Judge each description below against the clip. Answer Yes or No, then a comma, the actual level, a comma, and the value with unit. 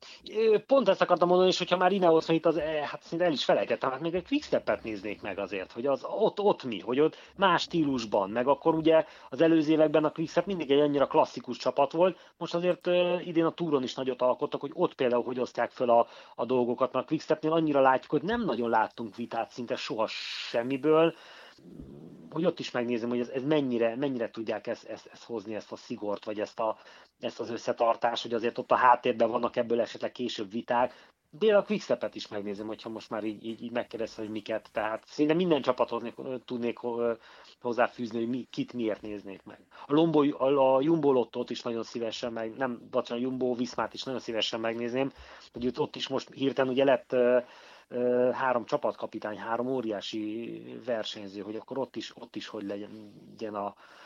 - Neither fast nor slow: No, fast, 190 wpm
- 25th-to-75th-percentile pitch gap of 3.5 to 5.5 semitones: Yes, average, 5.1 semitones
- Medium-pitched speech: No, low, 125 Hz